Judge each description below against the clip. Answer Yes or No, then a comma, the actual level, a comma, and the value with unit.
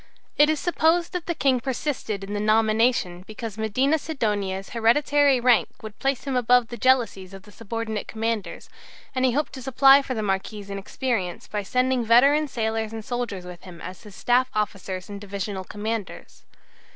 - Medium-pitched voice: No, high, 225 Hz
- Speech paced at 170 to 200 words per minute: Yes, average, 175 wpm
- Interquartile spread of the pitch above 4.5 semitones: No, average, 4.2 semitones